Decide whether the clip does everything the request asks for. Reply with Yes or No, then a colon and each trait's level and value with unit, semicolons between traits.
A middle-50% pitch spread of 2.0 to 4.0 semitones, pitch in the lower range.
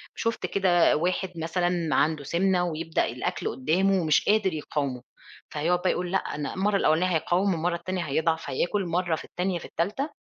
No: average, 2.8 semitones; medium, 175 Hz